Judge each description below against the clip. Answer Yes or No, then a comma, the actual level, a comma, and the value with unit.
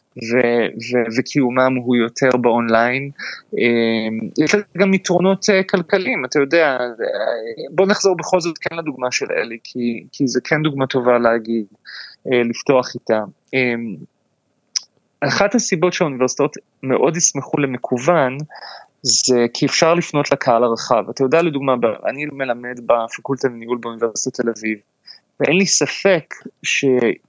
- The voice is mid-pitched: No, low, 130 Hz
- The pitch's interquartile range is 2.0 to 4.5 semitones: No, wide, 5.6 semitones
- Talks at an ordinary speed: Yes, average, 120 wpm